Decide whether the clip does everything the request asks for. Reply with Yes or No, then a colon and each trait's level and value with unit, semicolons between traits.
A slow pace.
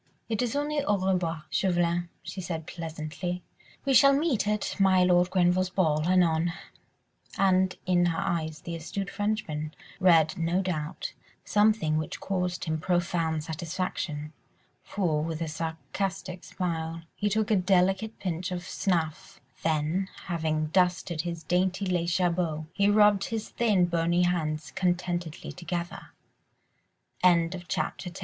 Yes: slow, 130 wpm